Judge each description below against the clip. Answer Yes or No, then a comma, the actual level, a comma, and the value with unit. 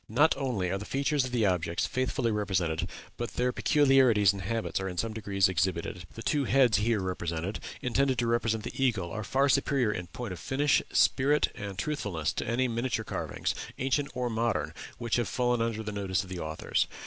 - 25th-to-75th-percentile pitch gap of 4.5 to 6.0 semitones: Yes, average, 5.1 semitones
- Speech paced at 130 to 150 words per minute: No, average, 195 wpm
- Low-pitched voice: Yes, low, 115 Hz